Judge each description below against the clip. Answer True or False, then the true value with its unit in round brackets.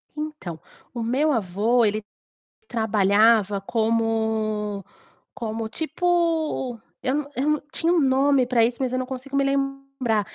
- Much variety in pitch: False (4.0 semitones)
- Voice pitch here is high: True (245 Hz)